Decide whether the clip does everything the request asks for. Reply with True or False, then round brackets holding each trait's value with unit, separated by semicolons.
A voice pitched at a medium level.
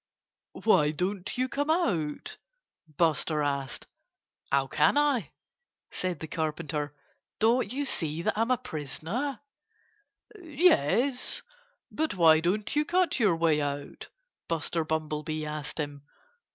True (165 Hz)